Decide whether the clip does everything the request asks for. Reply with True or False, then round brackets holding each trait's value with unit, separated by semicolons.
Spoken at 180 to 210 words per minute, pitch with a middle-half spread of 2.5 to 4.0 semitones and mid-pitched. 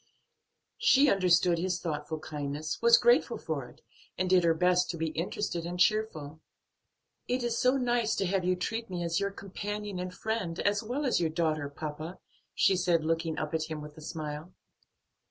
False (185 wpm; 4.6 semitones; 180 Hz)